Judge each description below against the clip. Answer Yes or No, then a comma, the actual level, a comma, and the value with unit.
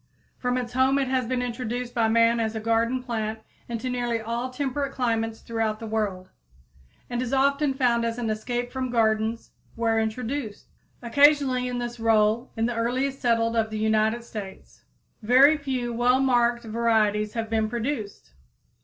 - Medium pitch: No, high, 235 Hz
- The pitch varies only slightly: Yes, narrow, 2.1 semitones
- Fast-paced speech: No, average, 165 wpm